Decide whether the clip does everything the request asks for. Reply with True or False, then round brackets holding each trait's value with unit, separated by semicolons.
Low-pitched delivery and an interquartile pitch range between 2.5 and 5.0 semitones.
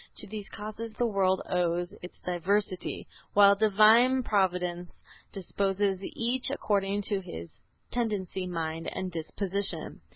False (195 Hz; 2.9 semitones)